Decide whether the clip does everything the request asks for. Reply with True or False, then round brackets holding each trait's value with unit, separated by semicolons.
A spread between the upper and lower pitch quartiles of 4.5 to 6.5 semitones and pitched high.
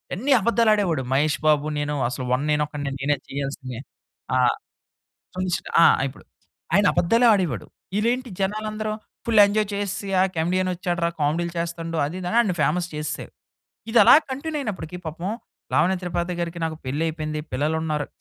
False (5.1 semitones; 170 Hz)